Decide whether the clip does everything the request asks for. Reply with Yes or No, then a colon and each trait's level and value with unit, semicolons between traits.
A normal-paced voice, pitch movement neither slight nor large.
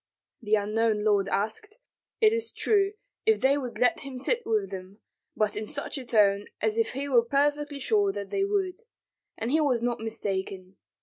No: average, 185 wpm; wide, 6.0 semitones